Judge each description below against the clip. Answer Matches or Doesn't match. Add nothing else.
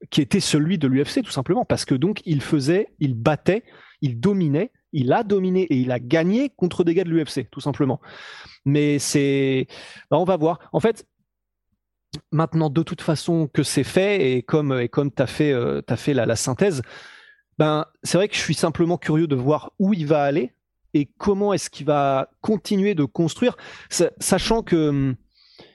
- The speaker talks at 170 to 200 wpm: Matches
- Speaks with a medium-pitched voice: Matches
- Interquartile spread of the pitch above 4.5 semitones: Matches